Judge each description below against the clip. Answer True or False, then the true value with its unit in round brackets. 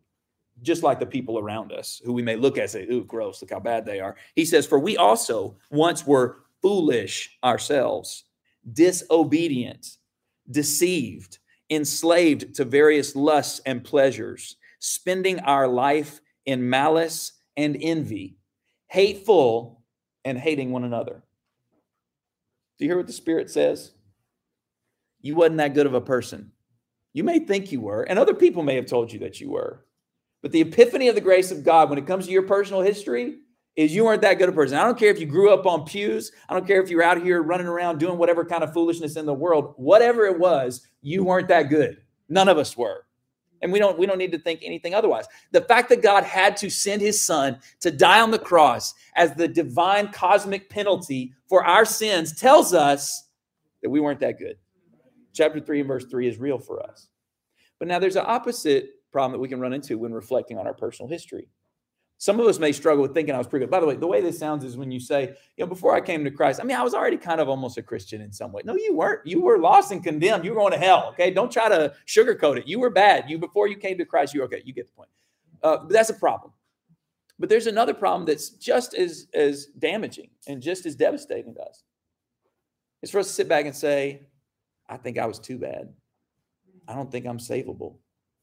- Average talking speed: False (215 wpm)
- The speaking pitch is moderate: True (165 Hz)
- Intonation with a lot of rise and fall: True (6.5 semitones)